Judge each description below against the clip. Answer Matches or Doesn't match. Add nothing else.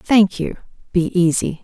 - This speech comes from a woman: Matches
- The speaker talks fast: Doesn't match